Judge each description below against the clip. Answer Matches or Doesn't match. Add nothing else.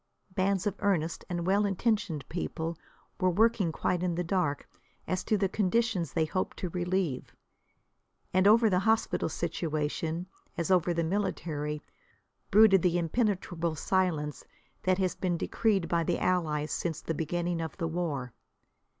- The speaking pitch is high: Doesn't match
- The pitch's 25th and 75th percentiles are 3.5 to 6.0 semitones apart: Doesn't match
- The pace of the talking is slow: Doesn't match